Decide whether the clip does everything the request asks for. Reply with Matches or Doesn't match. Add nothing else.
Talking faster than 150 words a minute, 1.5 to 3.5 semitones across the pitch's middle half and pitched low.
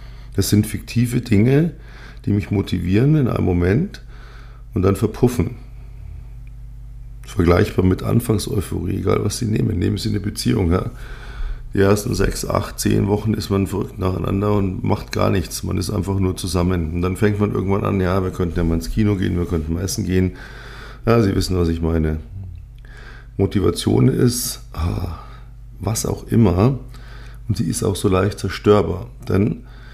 Doesn't match